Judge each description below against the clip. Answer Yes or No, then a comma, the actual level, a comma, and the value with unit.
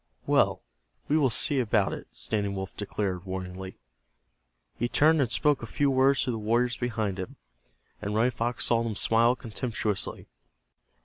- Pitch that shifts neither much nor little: Yes, average, 3.7 semitones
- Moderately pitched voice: No, low, 115 Hz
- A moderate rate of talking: Yes, average, 160 wpm